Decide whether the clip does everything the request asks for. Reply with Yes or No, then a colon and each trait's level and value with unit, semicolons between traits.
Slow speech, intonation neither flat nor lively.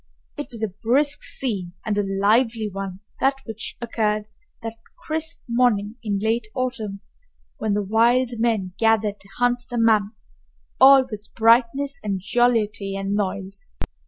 No: average, 145 wpm; average, 3.2 semitones